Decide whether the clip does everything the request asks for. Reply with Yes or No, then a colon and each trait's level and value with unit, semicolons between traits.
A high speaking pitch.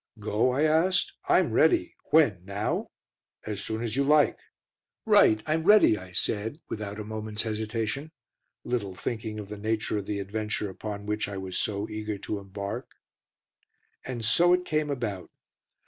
No: low, 110 Hz